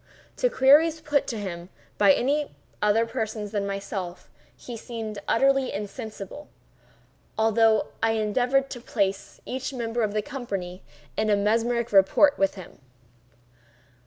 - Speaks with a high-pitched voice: Yes, high, 225 Hz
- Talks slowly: Yes, slow, 125 wpm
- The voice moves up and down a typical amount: Yes, average, 4.1 semitones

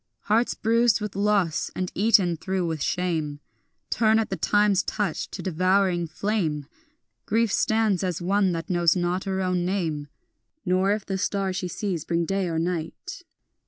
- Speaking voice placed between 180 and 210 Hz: Yes, medium, 185 Hz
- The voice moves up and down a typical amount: Yes, average, 3.1 semitones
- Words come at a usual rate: Yes, average, 160 wpm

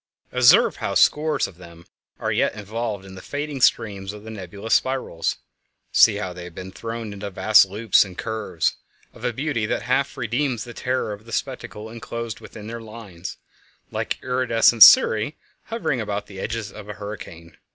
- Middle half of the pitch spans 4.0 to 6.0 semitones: No, average, 3.1 semitones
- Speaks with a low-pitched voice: Yes, low, 110 Hz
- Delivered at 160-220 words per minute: Yes, average, 170 wpm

